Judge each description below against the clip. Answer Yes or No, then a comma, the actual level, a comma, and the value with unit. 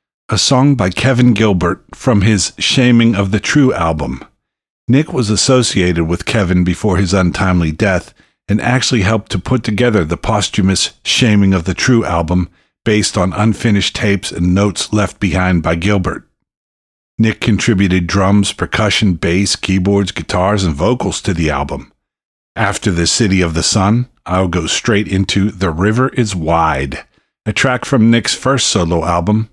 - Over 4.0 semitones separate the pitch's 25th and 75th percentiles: No, average, 3.7 semitones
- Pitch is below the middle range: Yes, low, 100 Hz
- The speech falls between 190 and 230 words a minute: No, average, 155 wpm